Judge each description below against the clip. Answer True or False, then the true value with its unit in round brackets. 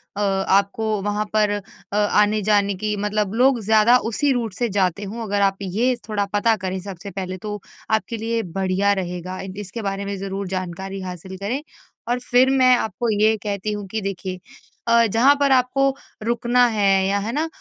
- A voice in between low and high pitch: False (205 Hz)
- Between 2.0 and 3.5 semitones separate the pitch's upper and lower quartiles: True (2.9 semitones)